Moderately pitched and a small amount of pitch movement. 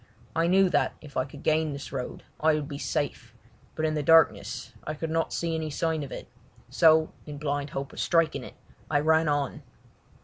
Yes: medium, 155 Hz; narrow, 1.9 semitones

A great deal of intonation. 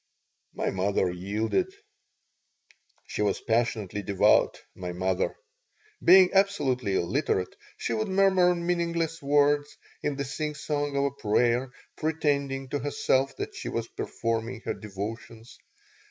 Yes: wide, 6.1 semitones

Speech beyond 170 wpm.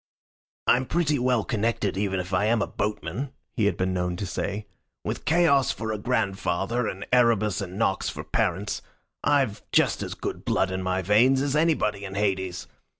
Yes: average, 180 wpm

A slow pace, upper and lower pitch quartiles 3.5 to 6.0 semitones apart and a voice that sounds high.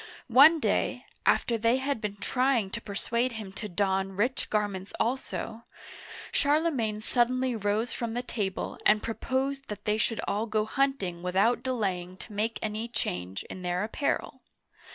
No: average, 155 wpm; average, 3.8 semitones; high, 220 Hz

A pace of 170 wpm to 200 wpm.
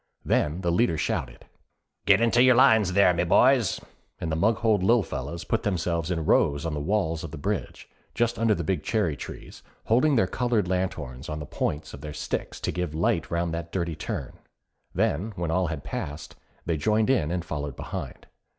Yes: average, 195 wpm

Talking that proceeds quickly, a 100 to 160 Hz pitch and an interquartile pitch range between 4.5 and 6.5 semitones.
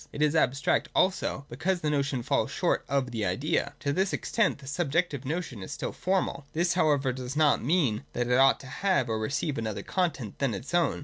Yes: fast, 210 wpm; medium, 140 Hz; average, 5.1 semitones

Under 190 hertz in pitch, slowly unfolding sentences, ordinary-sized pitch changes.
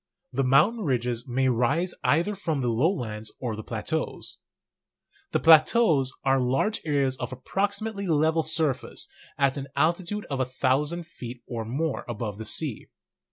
No: low, 135 Hz; average, 150 wpm; average, 4.8 semitones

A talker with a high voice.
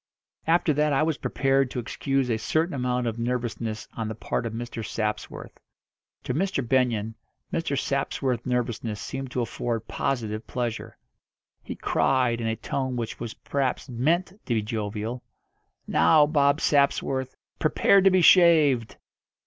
No: low, 125 Hz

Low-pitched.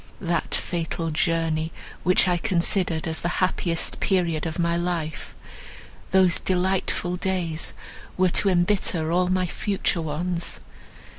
No: medium, 175 Hz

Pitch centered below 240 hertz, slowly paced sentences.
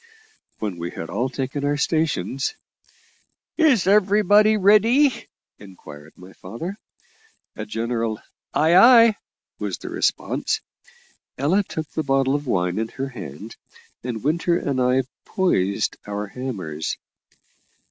Yes: low, 135 Hz; slow, 120 wpm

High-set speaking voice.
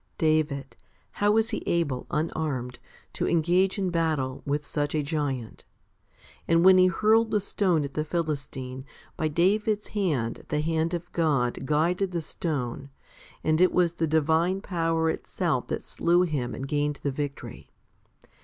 No: medium, 160 Hz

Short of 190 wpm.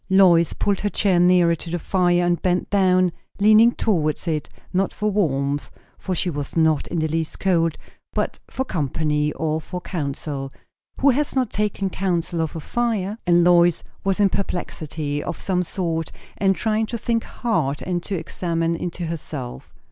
Yes: average, 170 wpm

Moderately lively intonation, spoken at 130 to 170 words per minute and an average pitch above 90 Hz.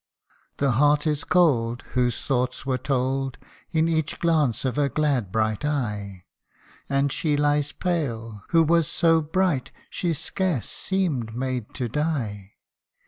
Yes: average, 4.7 semitones; average, 140 wpm; medium, 140 Hz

